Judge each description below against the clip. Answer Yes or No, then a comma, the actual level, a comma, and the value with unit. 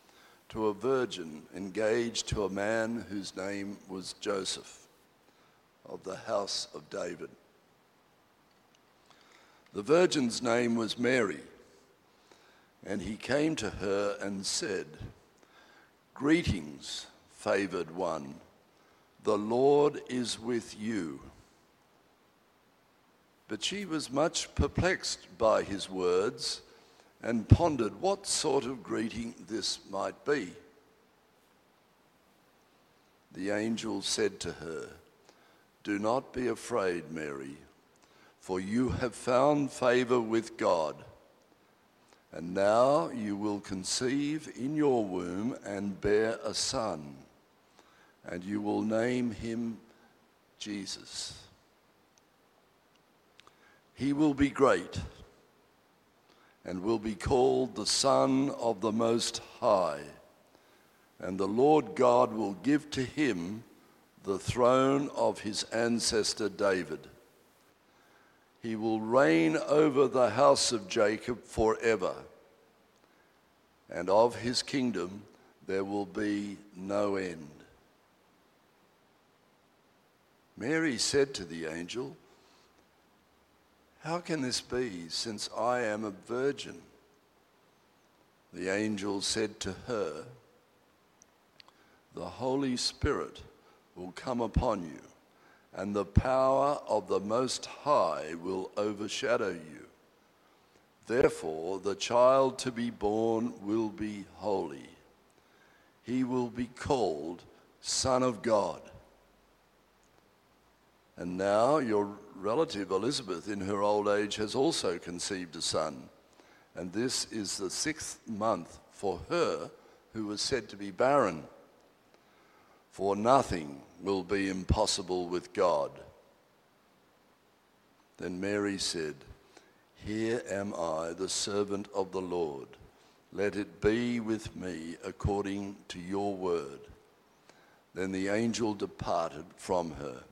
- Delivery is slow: Yes, slow, 105 wpm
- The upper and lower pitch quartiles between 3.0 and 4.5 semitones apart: Yes, average, 3.8 semitones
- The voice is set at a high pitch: No, low, 110 Hz